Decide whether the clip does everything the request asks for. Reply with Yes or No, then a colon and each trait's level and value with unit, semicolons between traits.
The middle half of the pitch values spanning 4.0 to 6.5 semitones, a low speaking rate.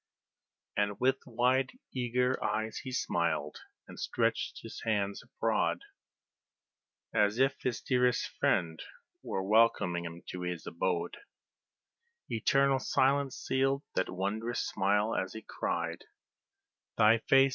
Yes: average, 5.2 semitones; slow, 115 wpm